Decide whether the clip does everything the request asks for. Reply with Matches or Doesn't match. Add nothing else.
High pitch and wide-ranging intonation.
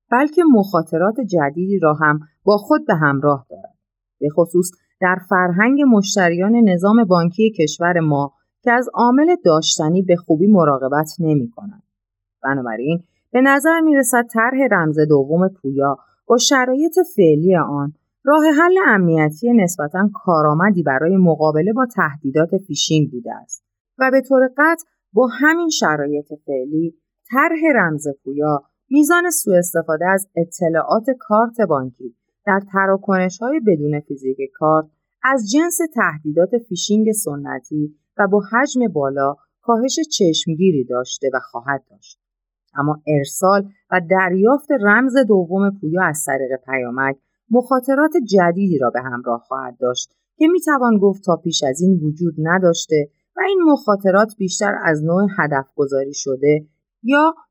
Doesn't match